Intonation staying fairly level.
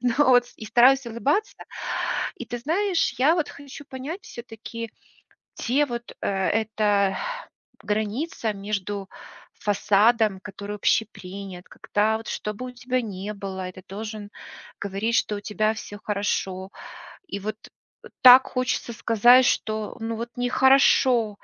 No: average, 3.5 semitones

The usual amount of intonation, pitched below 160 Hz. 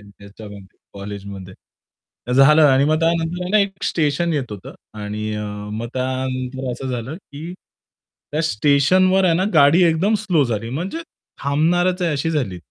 No: wide, 7.0 semitones; medium, 140 Hz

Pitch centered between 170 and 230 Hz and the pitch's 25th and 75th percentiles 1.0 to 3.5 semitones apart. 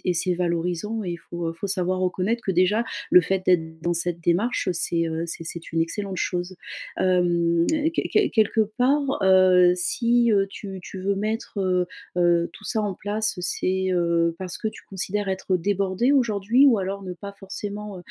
Yes: medium, 185 Hz; average, 3.0 semitones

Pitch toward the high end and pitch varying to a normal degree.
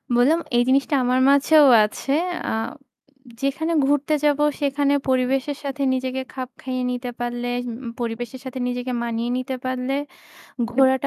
No: very high, 260 Hz; narrow, 2.0 semitones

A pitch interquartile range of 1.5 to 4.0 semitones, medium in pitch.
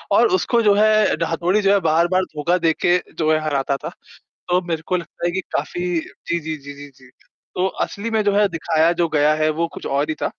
Yes: average, 3.5 semitones; medium, 170 Hz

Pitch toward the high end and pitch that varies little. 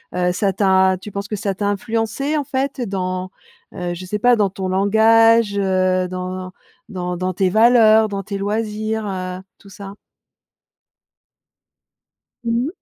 No: high, 200 Hz; average, 3.0 semitones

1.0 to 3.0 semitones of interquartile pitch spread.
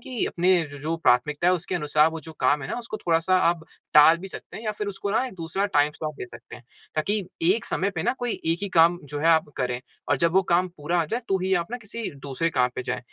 No: average, 4.4 semitones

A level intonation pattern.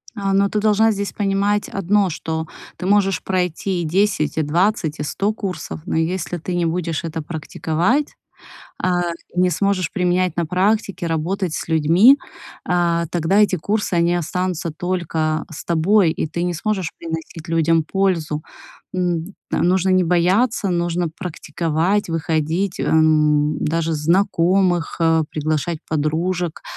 No: average, 3.1 semitones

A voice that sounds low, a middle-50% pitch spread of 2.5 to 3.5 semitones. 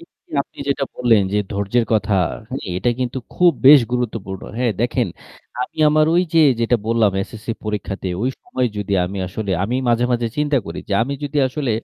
No: low, 120 Hz; average, 4.3 semitones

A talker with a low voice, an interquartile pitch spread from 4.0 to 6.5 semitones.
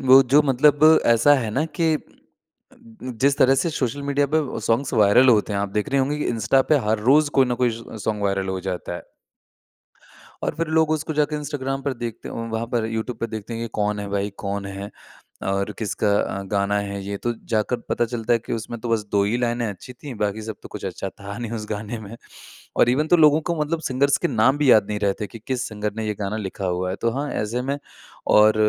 Yes: low, 115 Hz; average, 4.6 semitones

